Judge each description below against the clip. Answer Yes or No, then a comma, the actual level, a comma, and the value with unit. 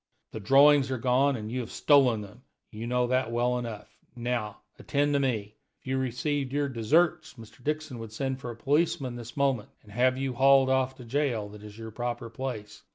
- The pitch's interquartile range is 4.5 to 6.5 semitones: No, average, 3.1 semitones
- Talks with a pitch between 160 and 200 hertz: No, low, 125 Hz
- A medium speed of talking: No, fast, 210 wpm